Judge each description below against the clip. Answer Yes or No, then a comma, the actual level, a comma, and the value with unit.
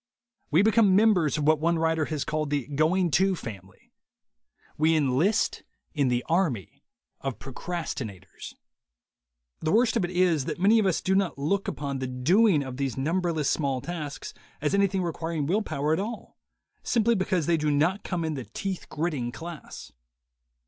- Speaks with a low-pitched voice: No, medium, 160 Hz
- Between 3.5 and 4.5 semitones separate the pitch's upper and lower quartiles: No, average, 4.9 semitones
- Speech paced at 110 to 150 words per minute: No, average, 170 wpm